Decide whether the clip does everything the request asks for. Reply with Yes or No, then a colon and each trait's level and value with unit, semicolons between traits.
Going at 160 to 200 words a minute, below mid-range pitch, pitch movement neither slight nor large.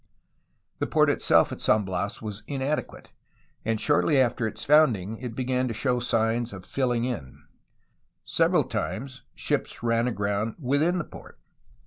No: average, 145 wpm; low, 120 Hz; average, 3.3 semitones